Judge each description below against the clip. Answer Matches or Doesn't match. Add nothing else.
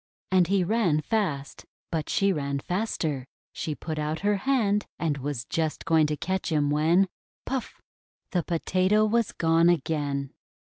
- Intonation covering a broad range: Doesn't match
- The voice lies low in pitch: Doesn't match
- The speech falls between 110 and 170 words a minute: Matches